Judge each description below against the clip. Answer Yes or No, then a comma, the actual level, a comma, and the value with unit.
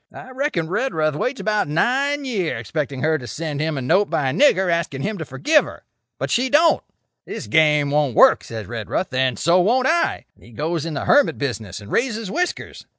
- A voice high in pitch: No, medium, 165 Hz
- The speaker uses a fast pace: Yes, fast, 210 wpm